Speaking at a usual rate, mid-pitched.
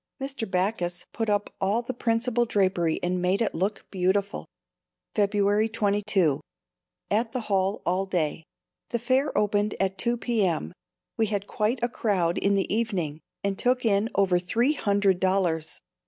No: average, 155 wpm; high, 200 Hz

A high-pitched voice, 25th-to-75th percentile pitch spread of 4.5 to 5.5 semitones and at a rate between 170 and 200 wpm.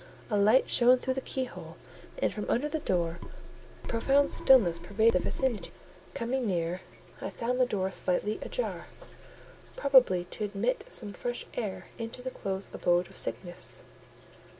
No: high, 220 Hz; average, 5.2 semitones; average, 150 wpm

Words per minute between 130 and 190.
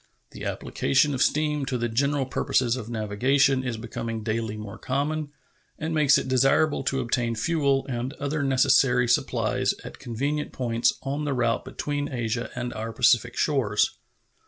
Yes: average, 155 wpm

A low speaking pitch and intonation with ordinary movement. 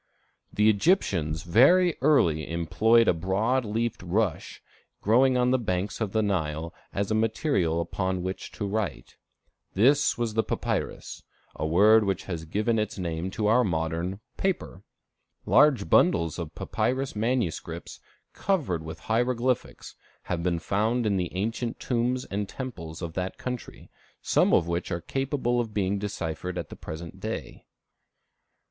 No: low, 105 Hz; wide, 5.7 semitones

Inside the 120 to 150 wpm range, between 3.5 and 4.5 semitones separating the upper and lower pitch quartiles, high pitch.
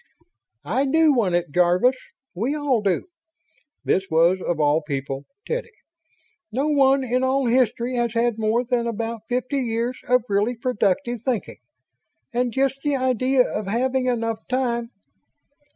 Yes: average, 145 wpm; average, 3.8 semitones; high, 240 Hz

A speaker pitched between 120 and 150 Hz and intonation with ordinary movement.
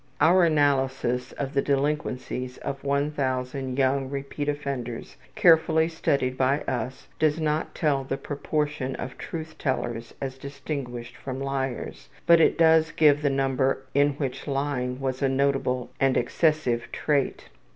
No: medium, 140 Hz; narrow, 2.2 semitones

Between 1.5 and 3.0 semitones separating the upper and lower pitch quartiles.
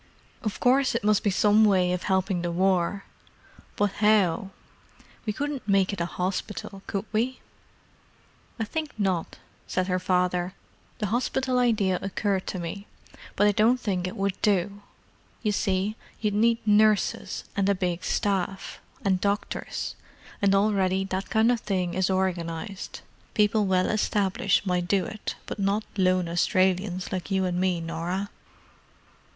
Yes: narrow, 2.4 semitones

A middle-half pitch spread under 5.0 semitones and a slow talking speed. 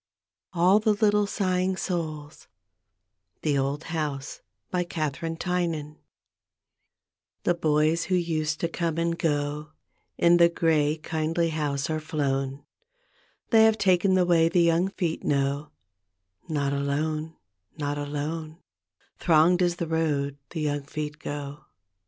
Yes: average, 2.8 semitones; slow, 130 wpm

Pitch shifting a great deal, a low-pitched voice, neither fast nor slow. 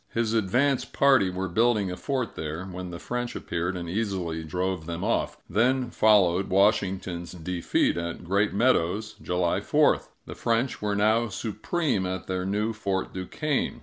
No: average, 4.0 semitones; very low, 95 Hz; average, 155 wpm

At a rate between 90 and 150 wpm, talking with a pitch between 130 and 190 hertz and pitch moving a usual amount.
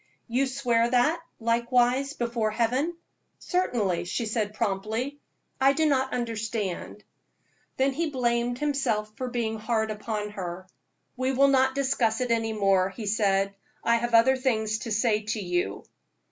No: average, 145 wpm; high, 235 Hz; average, 3.5 semitones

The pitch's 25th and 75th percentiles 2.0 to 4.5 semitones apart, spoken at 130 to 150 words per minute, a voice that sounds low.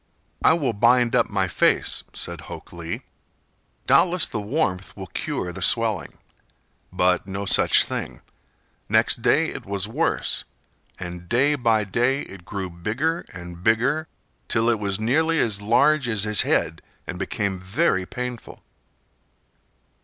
No: average, 5.2 semitones; average, 140 wpm; low, 105 Hz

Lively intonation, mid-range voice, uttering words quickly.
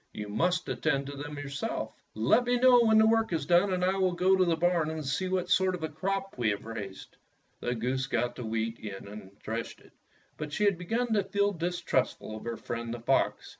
Yes: wide, 8.2 semitones; medium, 160 Hz; fast, 230 wpm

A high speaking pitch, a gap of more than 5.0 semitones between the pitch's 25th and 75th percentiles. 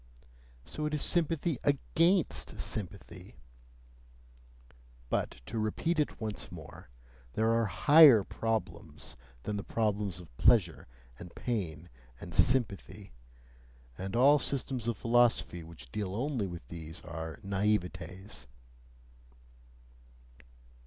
No: low, 105 Hz; wide, 5.6 semitones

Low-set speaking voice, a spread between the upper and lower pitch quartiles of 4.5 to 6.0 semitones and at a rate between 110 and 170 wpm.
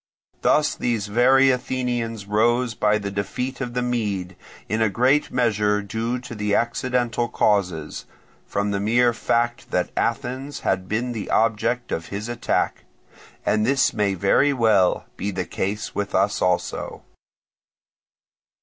No: low, 115 Hz; average, 3.2 semitones; average, 140 wpm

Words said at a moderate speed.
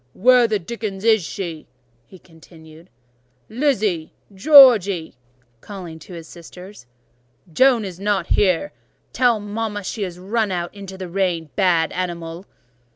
No: slow, 125 wpm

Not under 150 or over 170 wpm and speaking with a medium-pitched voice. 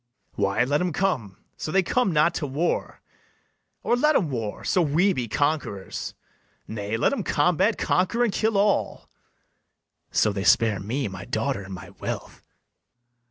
Yes: average, 160 wpm; medium, 145 Hz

